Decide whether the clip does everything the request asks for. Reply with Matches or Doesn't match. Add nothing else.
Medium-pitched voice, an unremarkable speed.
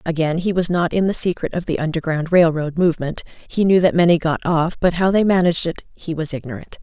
Doesn't match